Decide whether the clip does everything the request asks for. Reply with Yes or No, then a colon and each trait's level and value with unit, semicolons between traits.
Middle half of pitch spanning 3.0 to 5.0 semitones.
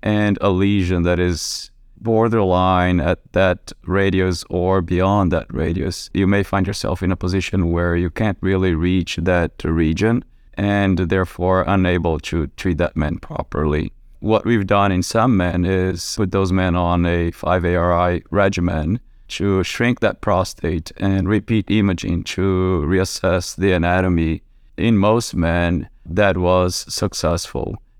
No: narrow, 2.4 semitones